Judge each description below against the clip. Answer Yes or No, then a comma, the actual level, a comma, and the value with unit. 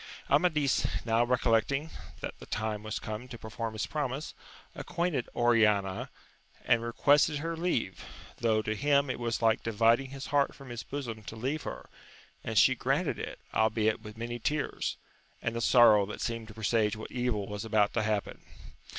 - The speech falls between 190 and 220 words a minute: No, average, 170 wpm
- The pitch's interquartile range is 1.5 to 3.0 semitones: No, average, 3.9 semitones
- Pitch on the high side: No, low, 115 Hz